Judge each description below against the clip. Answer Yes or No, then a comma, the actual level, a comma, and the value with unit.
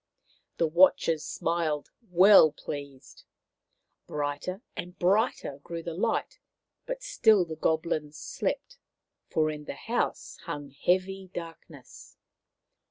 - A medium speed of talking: No, slow, 105 wpm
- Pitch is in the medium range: Yes, medium, 165 Hz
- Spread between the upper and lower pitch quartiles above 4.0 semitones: No, average, 3.6 semitones